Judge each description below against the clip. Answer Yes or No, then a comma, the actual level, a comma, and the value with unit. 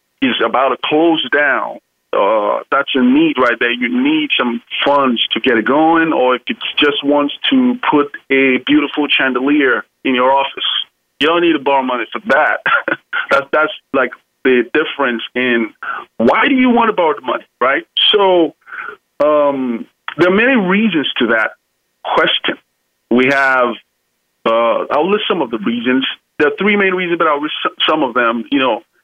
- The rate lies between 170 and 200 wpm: Yes, average, 180 wpm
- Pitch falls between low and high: Yes, medium, 145 Hz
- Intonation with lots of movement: Yes, wide, 8.0 semitones